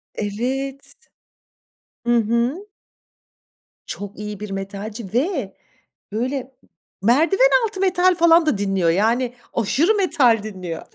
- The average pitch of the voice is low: No, high, 235 Hz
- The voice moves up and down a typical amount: No, wide, 7.6 semitones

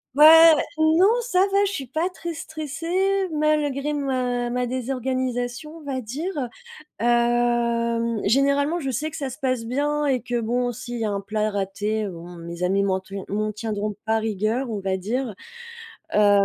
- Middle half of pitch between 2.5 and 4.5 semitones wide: No, wide, 5.5 semitones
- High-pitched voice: Yes, high, 245 Hz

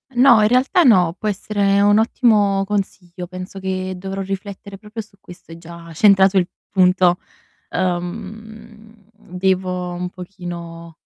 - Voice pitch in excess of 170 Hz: Yes, high, 190 Hz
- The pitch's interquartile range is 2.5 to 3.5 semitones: Yes, average, 2.8 semitones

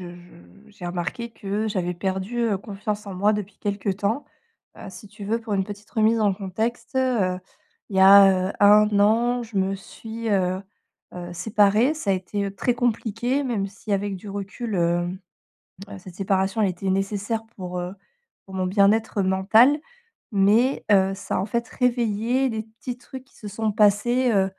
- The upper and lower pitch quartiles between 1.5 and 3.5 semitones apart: Yes, average, 2.9 semitones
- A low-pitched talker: No, high, 205 Hz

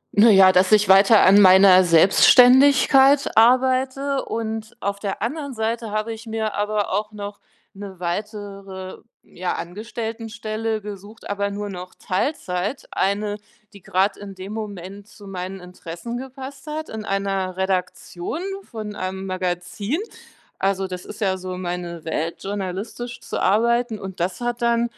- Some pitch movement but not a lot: Yes, average, 3.3 semitones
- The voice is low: No, high, 205 Hz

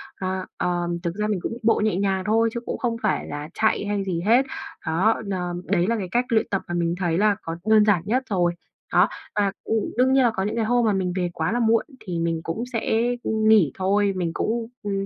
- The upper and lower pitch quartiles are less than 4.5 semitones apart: Yes, average, 3.9 semitones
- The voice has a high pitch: Yes, high, 200 Hz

